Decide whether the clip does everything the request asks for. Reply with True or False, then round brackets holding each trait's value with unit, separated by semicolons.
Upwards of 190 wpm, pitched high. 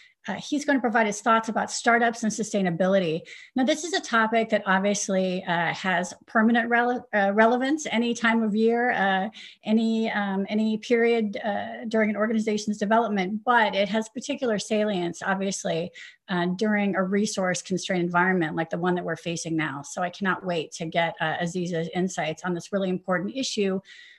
False (175 wpm; 210 Hz)